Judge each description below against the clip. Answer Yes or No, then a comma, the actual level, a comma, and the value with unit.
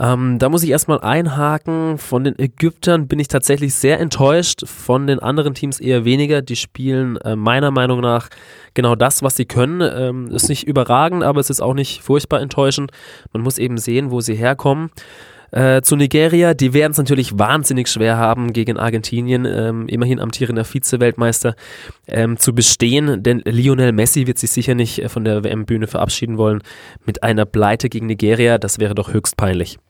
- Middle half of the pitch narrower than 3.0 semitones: No, average, 3.4 semitones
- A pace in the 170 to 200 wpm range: Yes, average, 180 wpm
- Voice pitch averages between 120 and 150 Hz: Yes, low, 125 Hz